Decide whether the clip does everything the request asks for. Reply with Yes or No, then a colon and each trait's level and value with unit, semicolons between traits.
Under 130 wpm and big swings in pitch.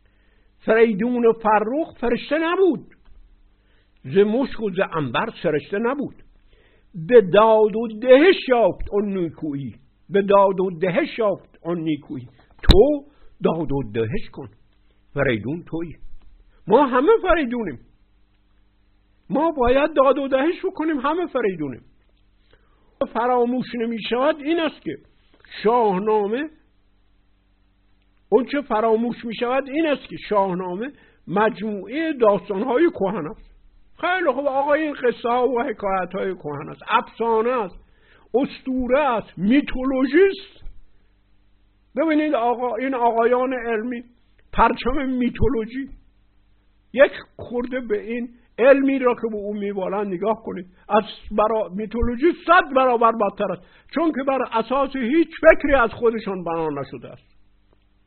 Yes: average, 120 wpm; wide, 8.9 semitones